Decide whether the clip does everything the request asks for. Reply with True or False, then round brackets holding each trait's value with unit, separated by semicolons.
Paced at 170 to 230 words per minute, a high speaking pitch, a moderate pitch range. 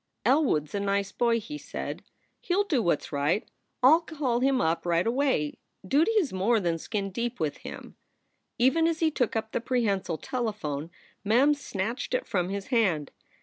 False (190 wpm; 230 Hz; 6.5 semitones)